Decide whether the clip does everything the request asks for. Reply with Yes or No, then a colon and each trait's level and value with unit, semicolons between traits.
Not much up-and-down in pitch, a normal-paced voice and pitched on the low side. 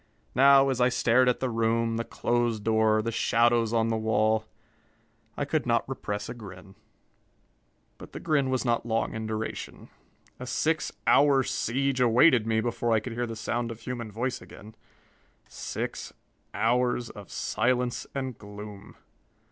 Yes: narrow, 2.2 semitones; average, 155 wpm; low, 115 Hz